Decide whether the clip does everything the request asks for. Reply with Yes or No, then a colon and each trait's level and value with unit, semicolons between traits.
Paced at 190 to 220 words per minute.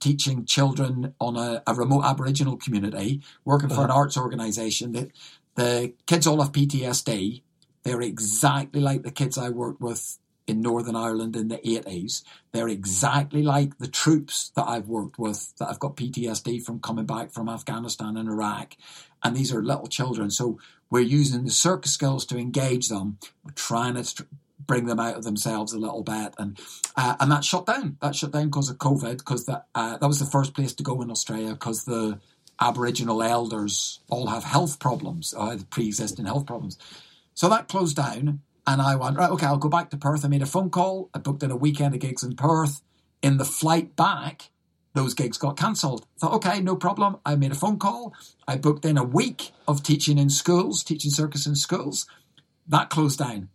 Yes: average, 195 wpm